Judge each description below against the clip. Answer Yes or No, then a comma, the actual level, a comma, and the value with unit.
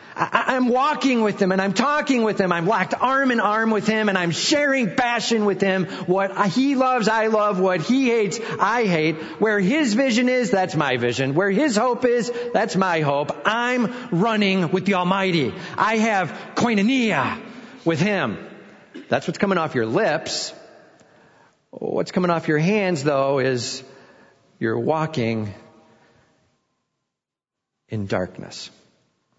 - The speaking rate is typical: Yes, average, 150 wpm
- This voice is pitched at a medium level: No, high, 200 Hz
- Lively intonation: Yes, wide, 6.0 semitones